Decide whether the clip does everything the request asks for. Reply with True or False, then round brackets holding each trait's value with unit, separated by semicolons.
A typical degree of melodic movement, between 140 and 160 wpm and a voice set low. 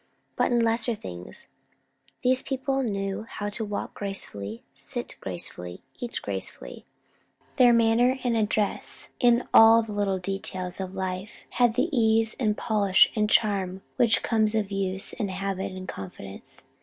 False (3.3 semitones; 145 wpm; 210 Hz)